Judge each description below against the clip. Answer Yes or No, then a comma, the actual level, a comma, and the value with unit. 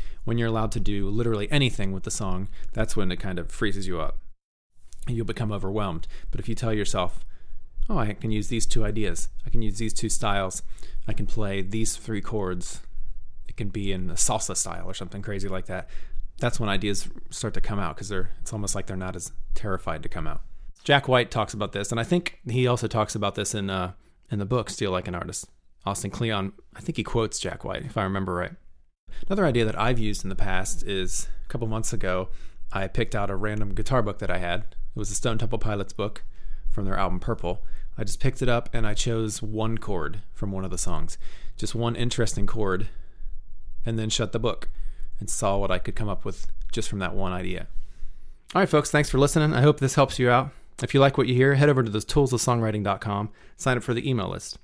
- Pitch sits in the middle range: No, low, 105 Hz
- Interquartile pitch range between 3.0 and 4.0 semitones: Yes, average, 3.4 semitones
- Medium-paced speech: No, fast, 230 wpm